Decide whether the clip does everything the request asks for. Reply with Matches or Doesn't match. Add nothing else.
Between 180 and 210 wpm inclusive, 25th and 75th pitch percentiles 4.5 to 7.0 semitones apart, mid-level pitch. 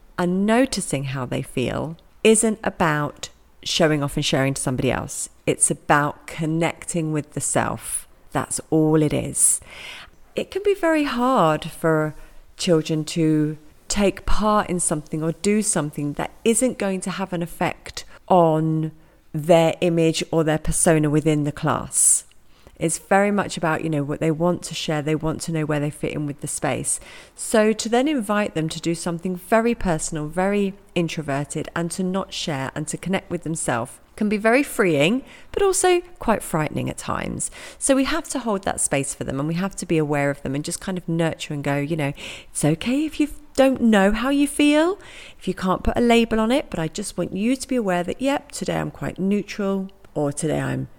Matches